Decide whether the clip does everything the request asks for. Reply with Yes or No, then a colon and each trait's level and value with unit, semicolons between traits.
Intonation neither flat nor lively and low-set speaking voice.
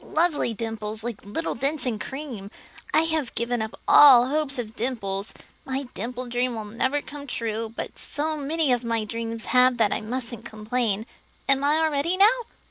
No: average, 4.2 semitones; high, 245 Hz